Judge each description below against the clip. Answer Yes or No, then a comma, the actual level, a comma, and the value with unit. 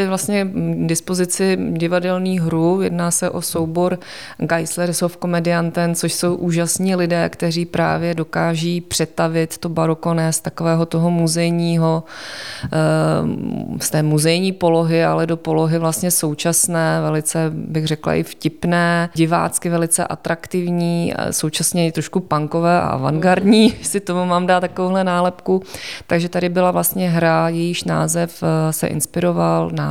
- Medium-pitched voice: Yes, medium, 170 Hz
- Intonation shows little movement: Yes, narrow, 1.5 semitones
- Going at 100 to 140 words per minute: Yes, average, 130 wpm